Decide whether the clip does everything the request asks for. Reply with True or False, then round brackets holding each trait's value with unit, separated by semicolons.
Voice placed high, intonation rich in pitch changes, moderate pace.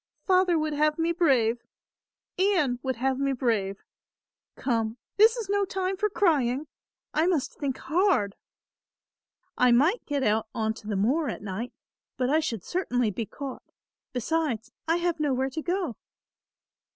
True (275 Hz; 6.3 semitones; 150 wpm)